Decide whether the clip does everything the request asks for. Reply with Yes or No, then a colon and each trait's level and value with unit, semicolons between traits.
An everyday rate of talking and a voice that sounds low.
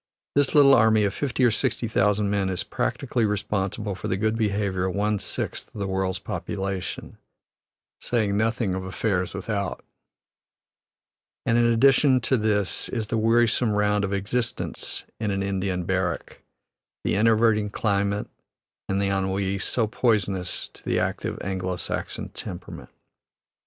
Yes: average, 145 wpm; low, 105 Hz